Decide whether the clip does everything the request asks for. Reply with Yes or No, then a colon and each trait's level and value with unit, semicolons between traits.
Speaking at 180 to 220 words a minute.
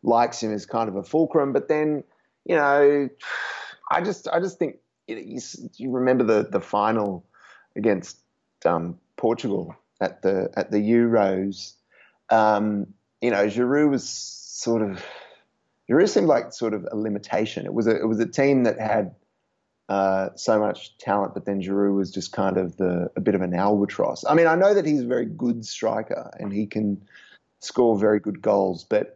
Yes: average, 185 wpm